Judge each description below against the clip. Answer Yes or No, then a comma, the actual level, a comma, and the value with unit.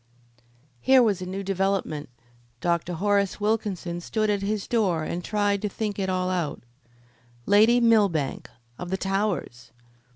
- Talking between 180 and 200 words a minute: No, average, 140 wpm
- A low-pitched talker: No, high, 195 Hz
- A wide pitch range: No, average, 3.0 semitones